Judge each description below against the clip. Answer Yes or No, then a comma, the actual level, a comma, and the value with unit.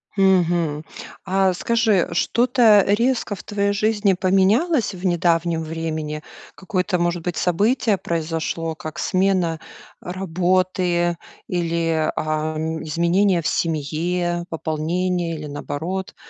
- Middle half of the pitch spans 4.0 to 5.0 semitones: No, average, 2.8 semitones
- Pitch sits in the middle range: Yes, medium, 175 Hz